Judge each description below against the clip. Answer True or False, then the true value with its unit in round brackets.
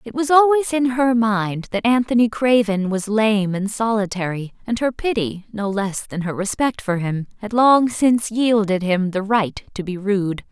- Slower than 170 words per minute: False (190 wpm)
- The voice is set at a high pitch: True (215 Hz)